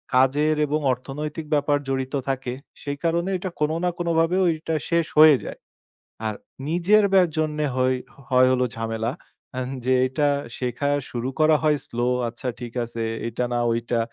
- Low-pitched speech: No, medium, 145 Hz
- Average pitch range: Yes, average, 3.9 semitones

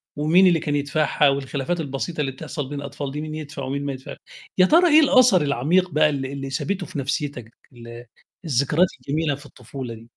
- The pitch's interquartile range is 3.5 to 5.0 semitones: No, average, 3.0 semitones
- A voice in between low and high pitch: Yes, medium, 145 Hz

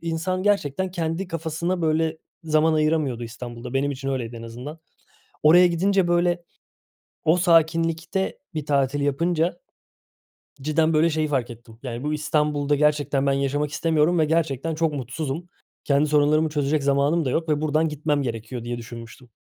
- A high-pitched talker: No, medium, 150 Hz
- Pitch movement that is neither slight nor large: Yes, average, 3.1 semitones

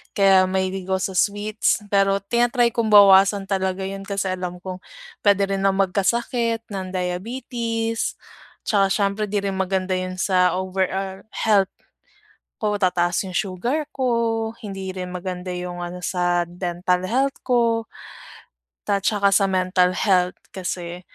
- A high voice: Yes, high, 195 Hz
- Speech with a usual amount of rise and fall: No, narrow, 2.3 semitones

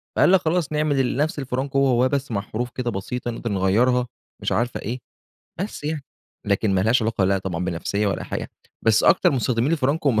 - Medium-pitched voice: No, low, 125 Hz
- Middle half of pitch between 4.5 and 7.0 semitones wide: Yes, average, 4.9 semitones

